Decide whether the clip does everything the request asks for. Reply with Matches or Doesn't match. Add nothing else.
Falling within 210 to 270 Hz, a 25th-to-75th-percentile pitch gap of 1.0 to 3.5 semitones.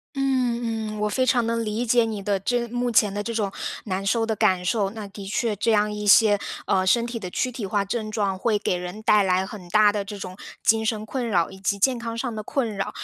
Matches